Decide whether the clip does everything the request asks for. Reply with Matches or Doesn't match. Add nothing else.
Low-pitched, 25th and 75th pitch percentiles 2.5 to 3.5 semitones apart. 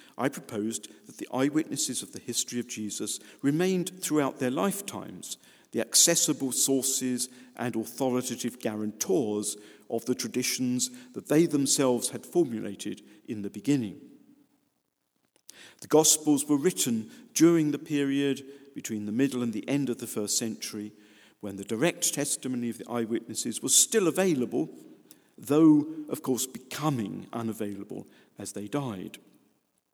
Doesn't match